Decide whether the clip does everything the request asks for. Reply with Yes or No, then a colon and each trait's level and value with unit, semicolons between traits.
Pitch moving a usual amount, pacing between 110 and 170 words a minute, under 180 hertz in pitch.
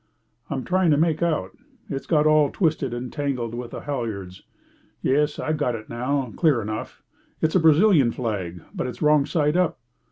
No: average, 4.7 semitones; average, 180 wpm; medium, 140 Hz